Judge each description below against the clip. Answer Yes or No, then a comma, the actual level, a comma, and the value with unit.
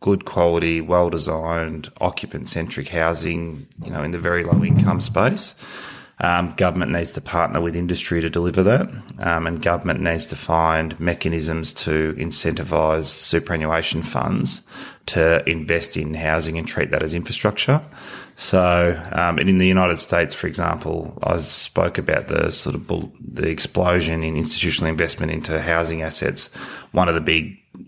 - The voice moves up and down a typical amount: No, narrow, 1.4 semitones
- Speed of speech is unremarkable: Yes, average, 145 wpm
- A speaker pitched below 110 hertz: Yes, very low, 85 Hz